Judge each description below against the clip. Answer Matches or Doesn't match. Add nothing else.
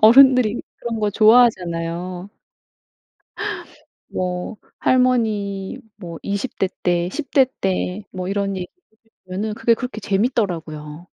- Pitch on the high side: Matches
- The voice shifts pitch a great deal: Doesn't match